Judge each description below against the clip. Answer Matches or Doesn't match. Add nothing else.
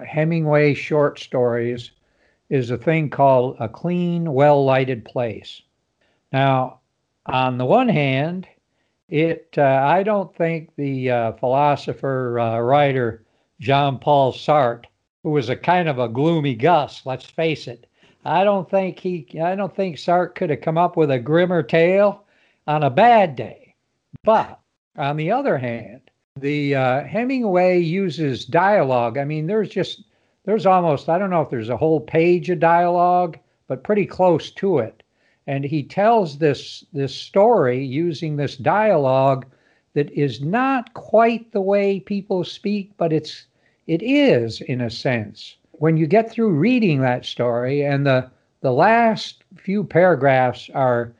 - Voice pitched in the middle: Matches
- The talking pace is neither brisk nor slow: Matches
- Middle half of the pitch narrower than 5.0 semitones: Doesn't match